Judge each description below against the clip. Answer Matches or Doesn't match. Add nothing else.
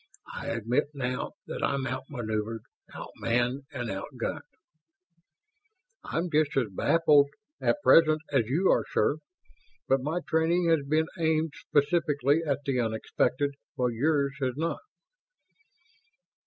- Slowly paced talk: Matches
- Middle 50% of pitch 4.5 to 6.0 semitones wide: Doesn't match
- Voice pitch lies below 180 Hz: Matches